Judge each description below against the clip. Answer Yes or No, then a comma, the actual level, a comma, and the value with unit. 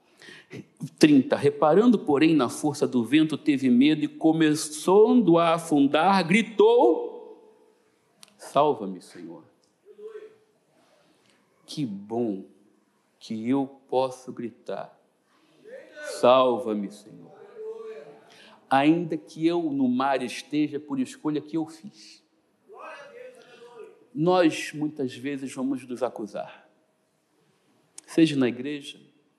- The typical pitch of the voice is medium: Yes, medium, 160 Hz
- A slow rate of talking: Yes, slow, 90 wpm